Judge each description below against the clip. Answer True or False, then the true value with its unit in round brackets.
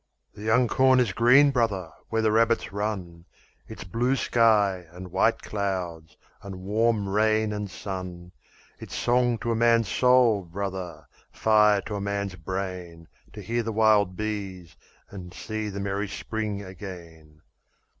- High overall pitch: False (100 Hz)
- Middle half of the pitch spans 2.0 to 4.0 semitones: True (3.3 semitones)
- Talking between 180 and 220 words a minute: False (145 wpm)